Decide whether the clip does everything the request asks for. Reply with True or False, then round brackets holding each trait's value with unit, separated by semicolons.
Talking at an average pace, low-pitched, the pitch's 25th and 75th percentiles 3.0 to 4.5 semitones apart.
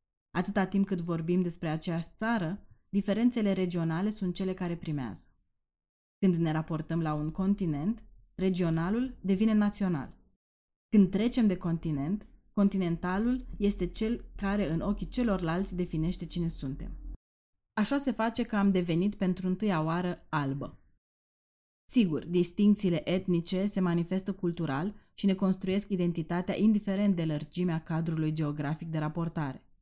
False (125 wpm; 180 Hz; 3.5 semitones)